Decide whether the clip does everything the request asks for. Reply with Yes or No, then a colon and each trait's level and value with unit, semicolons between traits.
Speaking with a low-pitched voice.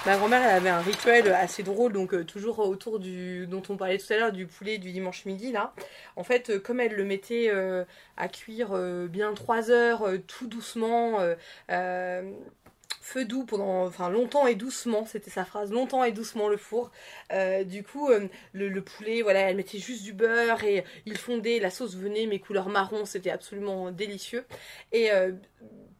No: high, 205 Hz